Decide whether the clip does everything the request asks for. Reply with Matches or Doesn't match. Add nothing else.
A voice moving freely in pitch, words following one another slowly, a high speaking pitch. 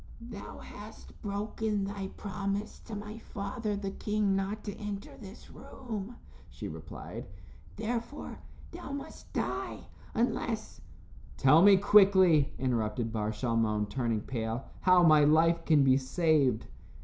Matches